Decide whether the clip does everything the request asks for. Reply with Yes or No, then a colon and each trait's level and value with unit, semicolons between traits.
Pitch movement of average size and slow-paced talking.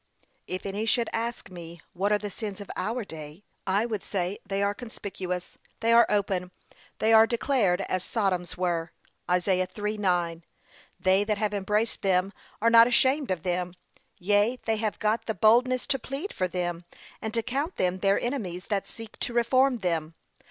No: average, 3.9 semitones; average, 175 wpm